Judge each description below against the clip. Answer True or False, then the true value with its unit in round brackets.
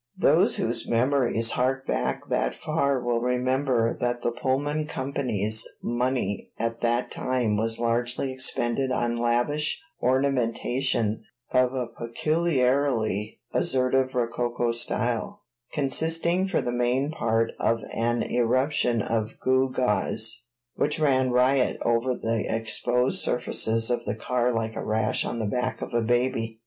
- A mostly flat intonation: True (2.3 semitones)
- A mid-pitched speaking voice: False (125 Hz)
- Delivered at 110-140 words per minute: True (135 wpm)